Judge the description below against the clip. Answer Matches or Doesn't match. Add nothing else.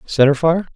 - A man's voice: Matches